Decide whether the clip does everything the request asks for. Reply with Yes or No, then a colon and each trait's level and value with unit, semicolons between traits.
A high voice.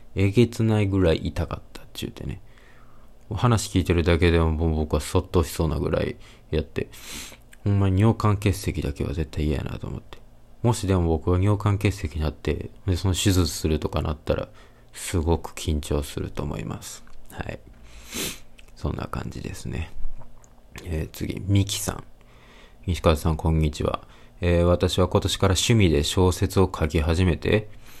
No: very low, 90 Hz